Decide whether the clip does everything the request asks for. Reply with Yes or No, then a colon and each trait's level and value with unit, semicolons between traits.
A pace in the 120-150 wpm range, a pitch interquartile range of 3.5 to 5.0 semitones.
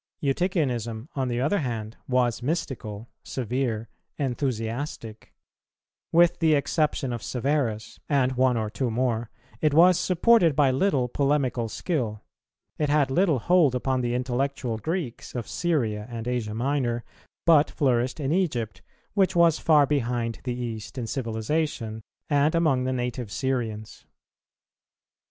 Yes: slow, 135 wpm; average, 4.2 semitones